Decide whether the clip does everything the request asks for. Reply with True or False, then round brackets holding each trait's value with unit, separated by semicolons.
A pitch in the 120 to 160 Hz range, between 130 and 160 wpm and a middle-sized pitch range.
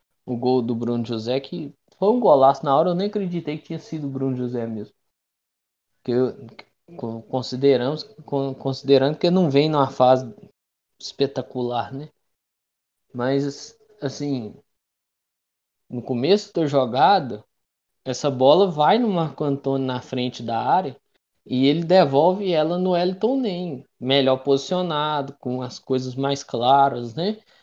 True (135 Hz; 140 wpm; 3.9 semitones)